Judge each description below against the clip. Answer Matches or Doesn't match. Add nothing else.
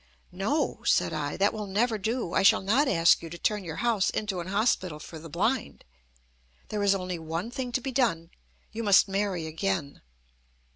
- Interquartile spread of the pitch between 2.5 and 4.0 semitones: Doesn't match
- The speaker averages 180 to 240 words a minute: Matches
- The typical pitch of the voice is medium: Doesn't match